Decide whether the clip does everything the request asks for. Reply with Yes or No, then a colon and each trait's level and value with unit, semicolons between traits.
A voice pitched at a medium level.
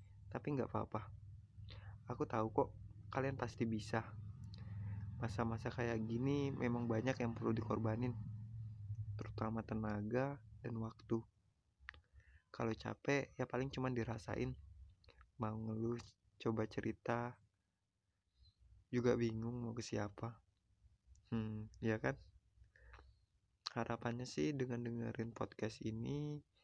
No: low, 110 Hz